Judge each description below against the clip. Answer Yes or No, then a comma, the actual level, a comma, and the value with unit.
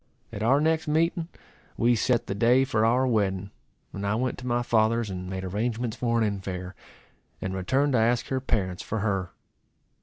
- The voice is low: Yes, low, 115 Hz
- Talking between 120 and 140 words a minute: No, average, 185 wpm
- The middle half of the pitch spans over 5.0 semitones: No, average, 4.2 semitones